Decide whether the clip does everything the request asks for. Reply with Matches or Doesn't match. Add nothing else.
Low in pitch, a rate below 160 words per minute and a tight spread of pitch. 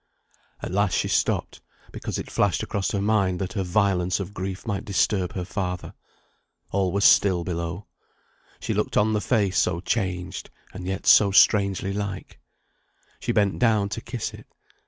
Doesn't match